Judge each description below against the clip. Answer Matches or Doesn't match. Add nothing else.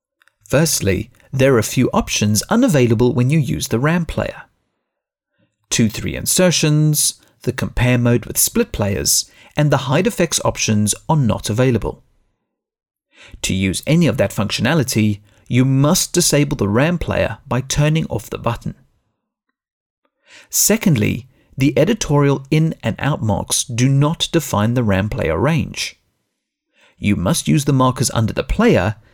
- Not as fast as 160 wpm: Matches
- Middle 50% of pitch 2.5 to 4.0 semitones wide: Doesn't match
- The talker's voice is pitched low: Matches